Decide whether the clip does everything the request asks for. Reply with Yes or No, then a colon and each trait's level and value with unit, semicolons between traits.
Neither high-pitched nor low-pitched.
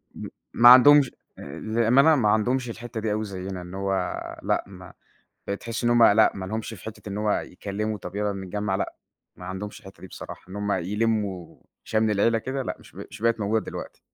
No: low, 105 Hz